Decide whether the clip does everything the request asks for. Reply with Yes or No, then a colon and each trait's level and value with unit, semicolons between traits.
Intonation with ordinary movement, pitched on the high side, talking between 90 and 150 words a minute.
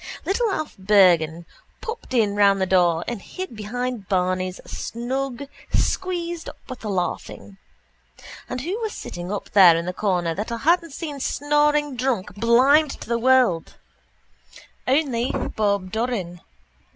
No: wide, 7.1 semitones; high, 230 Hz; average, 140 wpm